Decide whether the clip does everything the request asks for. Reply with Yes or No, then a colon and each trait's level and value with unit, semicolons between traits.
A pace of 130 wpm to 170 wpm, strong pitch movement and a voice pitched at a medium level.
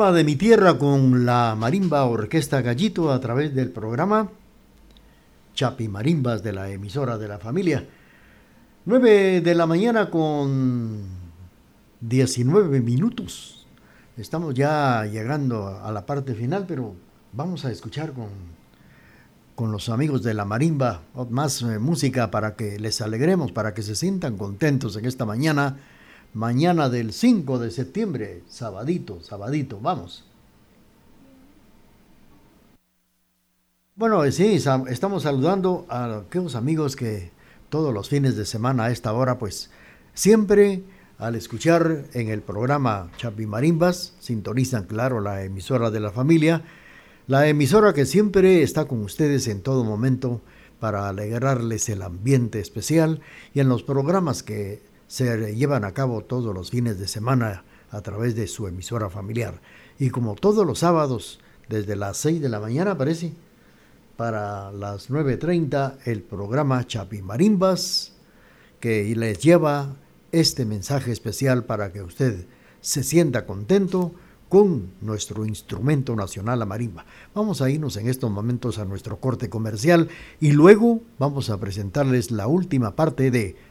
No: average, 135 wpm; wide, 6.1 semitones; low, 125 Hz